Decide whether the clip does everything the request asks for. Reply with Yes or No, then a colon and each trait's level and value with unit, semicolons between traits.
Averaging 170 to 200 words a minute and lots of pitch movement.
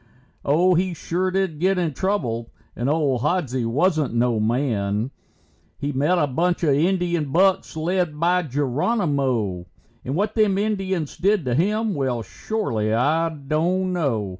No: average, 145 wpm; wide, 6.1 semitones